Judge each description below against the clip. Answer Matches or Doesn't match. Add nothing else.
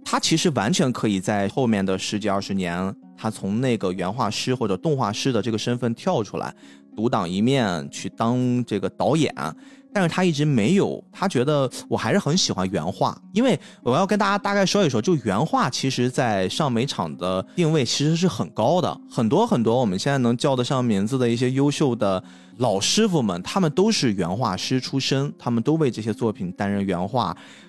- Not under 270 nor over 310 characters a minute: Matches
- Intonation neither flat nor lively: Doesn't match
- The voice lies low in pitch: Matches